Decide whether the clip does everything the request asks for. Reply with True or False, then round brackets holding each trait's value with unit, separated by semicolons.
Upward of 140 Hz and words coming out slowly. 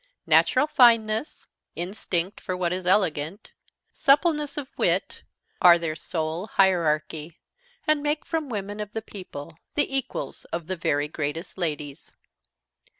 True (185 Hz; 130 wpm)